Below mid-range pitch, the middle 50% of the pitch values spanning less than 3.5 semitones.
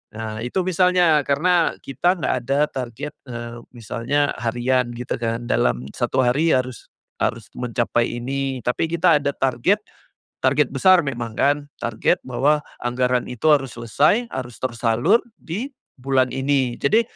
No: low, 130 Hz; average, 3.9 semitones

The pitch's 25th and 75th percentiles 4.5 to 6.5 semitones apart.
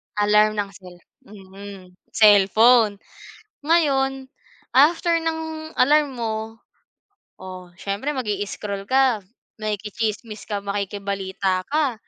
Yes: average, 5.1 semitones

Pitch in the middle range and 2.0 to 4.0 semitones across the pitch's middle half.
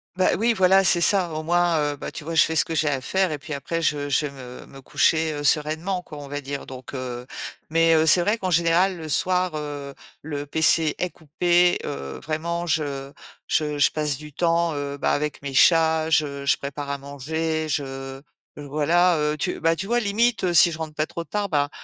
Yes: medium, 155 Hz; average, 3.1 semitones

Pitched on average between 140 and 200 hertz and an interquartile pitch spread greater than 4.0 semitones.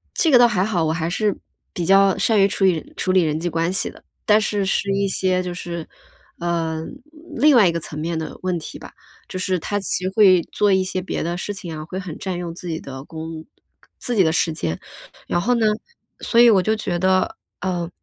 No: medium, 185 Hz; average, 3.0 semitones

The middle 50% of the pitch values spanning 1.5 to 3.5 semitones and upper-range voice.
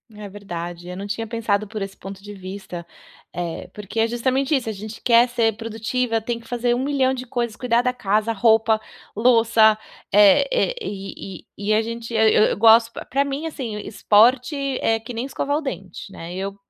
Yes: average, 3.2 semitones; high, 225 Hz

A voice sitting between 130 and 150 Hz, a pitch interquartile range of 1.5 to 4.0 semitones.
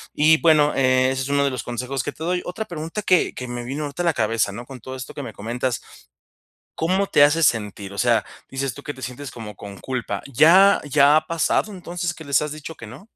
No: medium, 140 Hz; average, 4.7 semitones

